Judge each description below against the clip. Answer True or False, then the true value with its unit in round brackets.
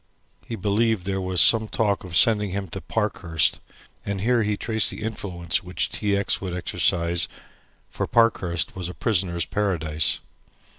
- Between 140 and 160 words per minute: True (155 wpm)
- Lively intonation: False (3.4 semitones)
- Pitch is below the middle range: True (95 Hz)